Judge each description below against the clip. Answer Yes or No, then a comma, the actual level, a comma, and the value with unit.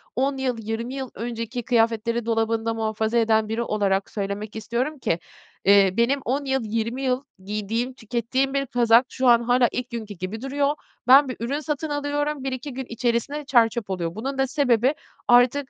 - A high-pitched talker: Yes, high, 235 Hz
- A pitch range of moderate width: Yes, average, 3.1 semitones